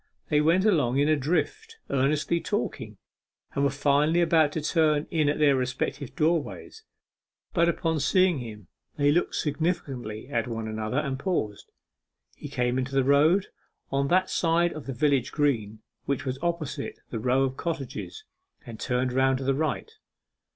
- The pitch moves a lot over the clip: No, average, 3.9 semitones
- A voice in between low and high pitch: Yes, medium, 145 Hz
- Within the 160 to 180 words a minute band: Yes, average, 165 wpm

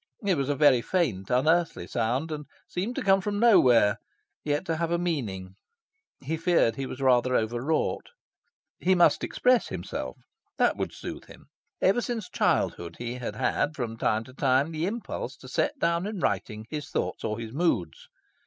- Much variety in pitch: Yes, wide, 7.0 semitones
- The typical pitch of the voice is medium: Yes, medium, 145 Hz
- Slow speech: No, average, 180 wpm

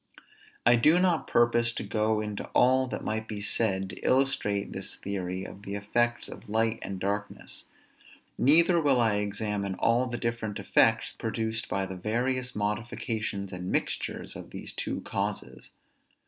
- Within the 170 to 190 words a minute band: No, average, 155 wpm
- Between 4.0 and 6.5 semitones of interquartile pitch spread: No, average, 3.0 semitones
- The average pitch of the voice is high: No, low, 110 Hz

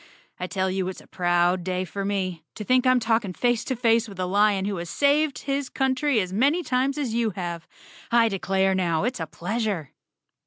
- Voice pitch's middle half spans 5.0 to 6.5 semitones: Yes, average, 5.3 semitones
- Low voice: No, high, 205 Hz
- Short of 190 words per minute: No, fast, 205 wpm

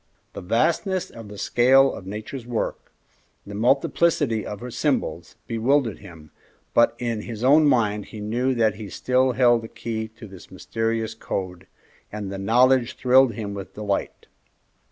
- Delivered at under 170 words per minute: Yes, average, 155 wpm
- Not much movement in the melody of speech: No, average, 3.5 semitones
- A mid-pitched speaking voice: No, low, 115 Hz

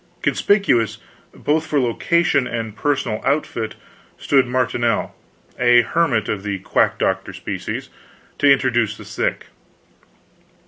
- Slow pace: Yes, slow, 110 wpm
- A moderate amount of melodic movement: Yes, average, 4.1 semitones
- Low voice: Yes, low, 125 Hz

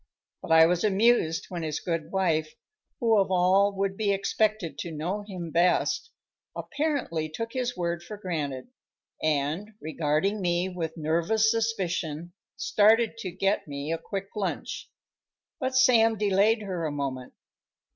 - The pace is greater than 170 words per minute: No, average, 145 wpm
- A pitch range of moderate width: Yes, average, 4.7 semitones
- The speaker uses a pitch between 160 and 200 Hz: Yes, medium, 185 Hz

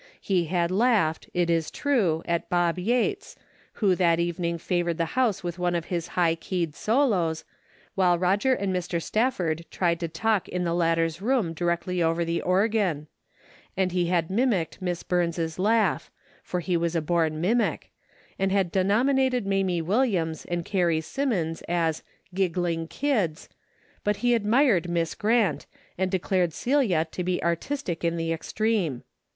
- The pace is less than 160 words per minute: No, average, 165 wpm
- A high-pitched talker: No, medium, 180 Hz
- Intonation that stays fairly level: No, average, 3.5 semitones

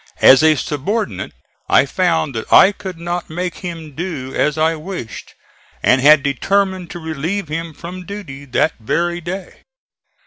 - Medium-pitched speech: Yes, medium, 165 Hz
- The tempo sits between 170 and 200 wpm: No, average, 150 wpm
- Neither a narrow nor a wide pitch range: Yes, average, 4.2 semitones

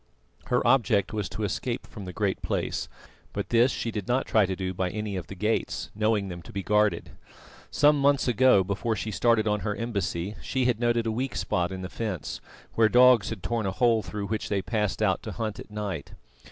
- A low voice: Yes, low, 105 Hz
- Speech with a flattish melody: No, average, 3.1 semitones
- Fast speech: Yes, fast, 220 wpm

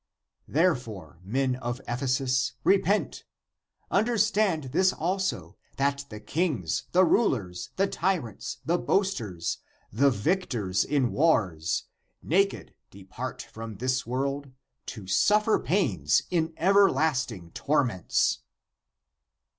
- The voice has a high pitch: No, low, 135 Hz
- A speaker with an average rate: No, slow, 105 wpm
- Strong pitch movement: Yes, wide, 8.8 semitones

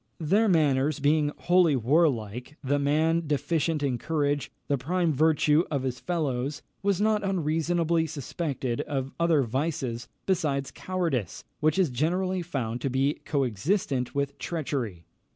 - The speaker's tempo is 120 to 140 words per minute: Yes, slow, 135 wpm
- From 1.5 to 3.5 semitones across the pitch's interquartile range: No, average, 4.0 semitones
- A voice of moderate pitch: Yes, medium, 150 Hz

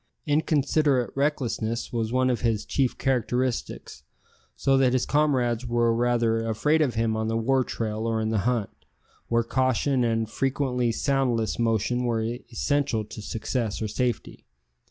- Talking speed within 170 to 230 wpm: No, average, 150 wpm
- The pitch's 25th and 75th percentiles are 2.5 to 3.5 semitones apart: Yes, average, 2.8 semitones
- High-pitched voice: No, low, 120 Hz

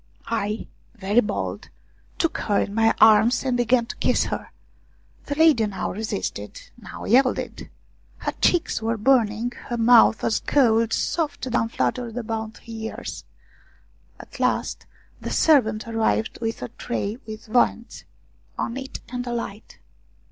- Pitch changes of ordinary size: No, narrow, 2.0 semitones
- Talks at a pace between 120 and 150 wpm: Yes, average, 140 wpm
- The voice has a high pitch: Yes, high, 230 Hz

